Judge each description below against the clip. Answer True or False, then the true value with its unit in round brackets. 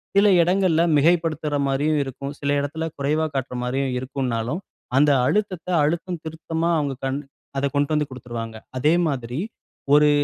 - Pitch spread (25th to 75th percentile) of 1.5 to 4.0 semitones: True (3.3 semitones)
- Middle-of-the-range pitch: True (145 Hz)